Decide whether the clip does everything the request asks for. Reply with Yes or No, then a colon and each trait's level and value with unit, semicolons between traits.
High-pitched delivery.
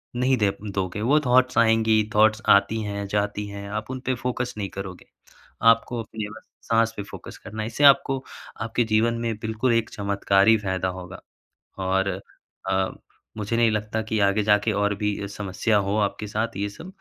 No: low, 105 Hz